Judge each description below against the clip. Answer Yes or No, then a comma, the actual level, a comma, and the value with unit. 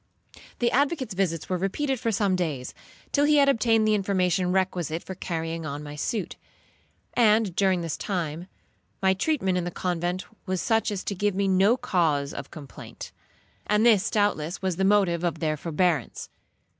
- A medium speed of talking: Yes, average, 170 wpm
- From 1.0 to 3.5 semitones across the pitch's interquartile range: No, average, 4.0 semitones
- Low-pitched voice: No, medium, 185 Hz